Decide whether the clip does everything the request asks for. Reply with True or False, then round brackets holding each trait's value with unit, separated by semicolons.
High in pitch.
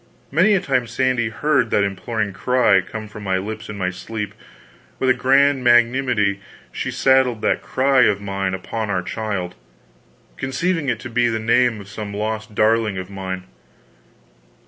False (110 Hz)